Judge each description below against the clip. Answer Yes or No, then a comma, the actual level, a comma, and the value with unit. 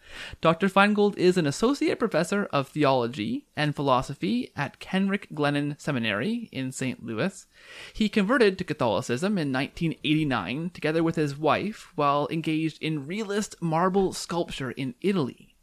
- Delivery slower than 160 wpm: Yes, slow, 135 wpm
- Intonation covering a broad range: Yes, wide, 5.8 semitones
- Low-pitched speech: No, medium, 165 Hz